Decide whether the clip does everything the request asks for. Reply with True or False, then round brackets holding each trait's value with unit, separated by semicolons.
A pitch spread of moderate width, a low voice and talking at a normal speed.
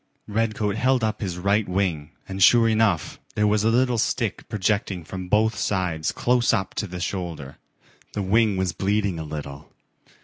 True (3.5 semitones; 100 Hz; 170 wpm)